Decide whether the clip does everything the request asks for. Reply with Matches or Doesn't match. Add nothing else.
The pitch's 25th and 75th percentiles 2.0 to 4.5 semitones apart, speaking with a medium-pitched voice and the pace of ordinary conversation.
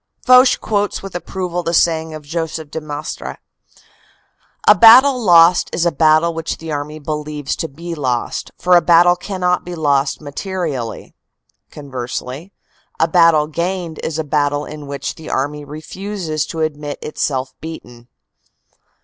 Matches